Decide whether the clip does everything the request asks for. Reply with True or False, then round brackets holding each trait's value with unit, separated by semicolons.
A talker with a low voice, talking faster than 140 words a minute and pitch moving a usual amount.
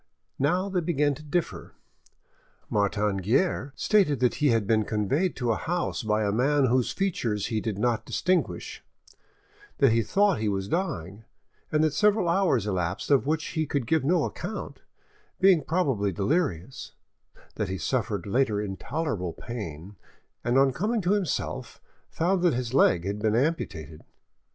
False (130 Hz; 155 wpm; 7.9 semitones)